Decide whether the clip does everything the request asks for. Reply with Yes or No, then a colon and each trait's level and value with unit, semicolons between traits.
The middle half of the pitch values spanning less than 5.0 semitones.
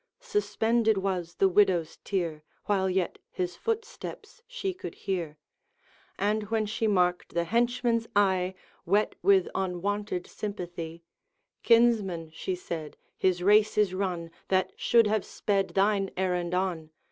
Yes: average, 3.3 semitones